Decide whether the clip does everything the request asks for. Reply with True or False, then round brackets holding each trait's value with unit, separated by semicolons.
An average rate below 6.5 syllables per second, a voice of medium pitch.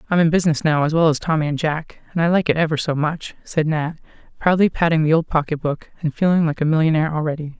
False (6.6 syllables/s; 155 Hz)